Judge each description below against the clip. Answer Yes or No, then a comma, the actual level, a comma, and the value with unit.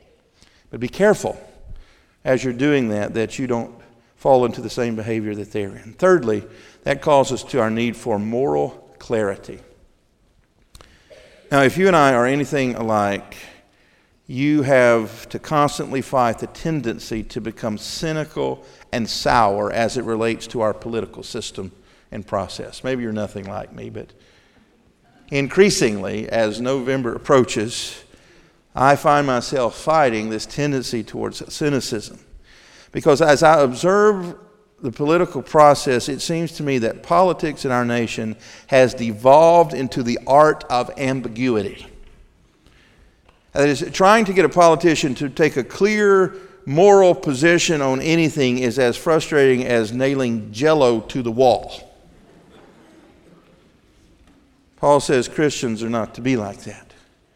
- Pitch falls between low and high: No, low, 130 Hz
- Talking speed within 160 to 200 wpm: No, slow, 135 wpm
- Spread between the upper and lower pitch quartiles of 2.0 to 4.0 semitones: No, average, 4.7 semitones